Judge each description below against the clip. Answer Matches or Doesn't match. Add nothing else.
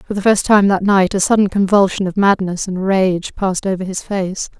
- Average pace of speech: Doesn't match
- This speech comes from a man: Doesn't match